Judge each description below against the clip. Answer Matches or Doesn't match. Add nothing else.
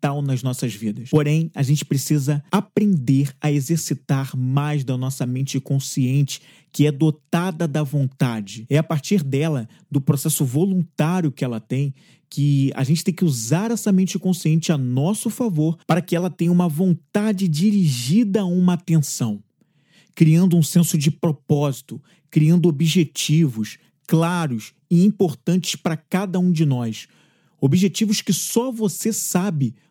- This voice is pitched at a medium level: Matches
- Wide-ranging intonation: Doesn't match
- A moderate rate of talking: Matches